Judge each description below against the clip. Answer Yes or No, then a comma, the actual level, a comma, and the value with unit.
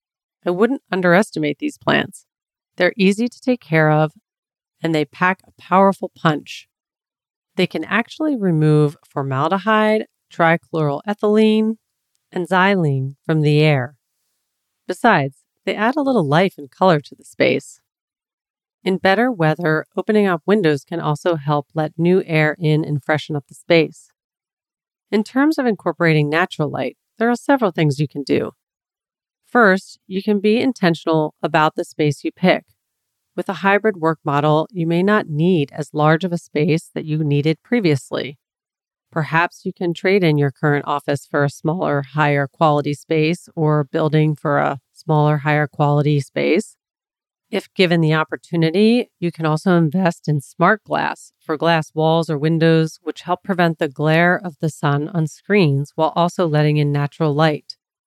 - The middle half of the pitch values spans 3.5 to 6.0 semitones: Yes, average, 3.8 semitones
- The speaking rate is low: No, average, 155 wpm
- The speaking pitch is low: No, medium, 160 Hz